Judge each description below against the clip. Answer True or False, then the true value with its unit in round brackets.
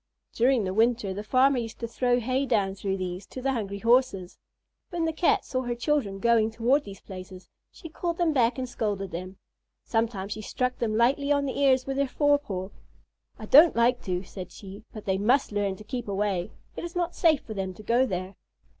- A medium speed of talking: False (210 wpm)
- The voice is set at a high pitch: True (230 Hz)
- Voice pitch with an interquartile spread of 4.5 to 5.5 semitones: True (5.2 semitones)